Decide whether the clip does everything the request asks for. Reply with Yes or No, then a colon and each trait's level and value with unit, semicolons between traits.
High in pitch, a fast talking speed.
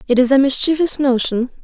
No: very high, 265 Hz; average, 185 wpm